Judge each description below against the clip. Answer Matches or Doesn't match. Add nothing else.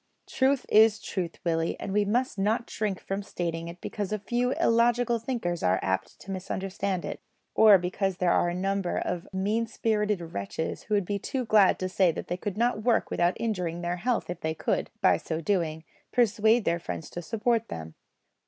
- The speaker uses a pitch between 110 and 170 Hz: Doesn't match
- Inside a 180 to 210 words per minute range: Matches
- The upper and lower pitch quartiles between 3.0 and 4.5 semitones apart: Matches